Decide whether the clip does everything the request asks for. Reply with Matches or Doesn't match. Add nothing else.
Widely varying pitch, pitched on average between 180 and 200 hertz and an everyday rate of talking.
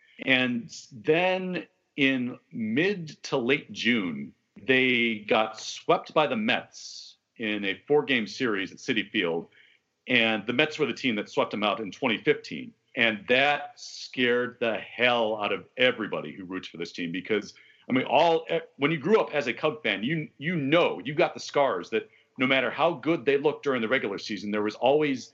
Doesn't match